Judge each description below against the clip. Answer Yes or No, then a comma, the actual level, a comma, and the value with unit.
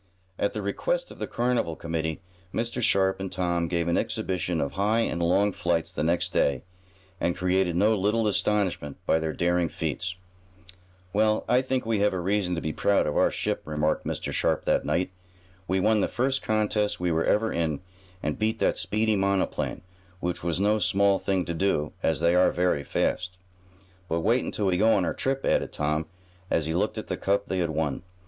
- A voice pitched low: Yes, very low, 95 Hz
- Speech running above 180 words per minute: Yes, average, 195 wpm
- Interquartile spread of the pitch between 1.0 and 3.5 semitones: No, average, 3.9 semitones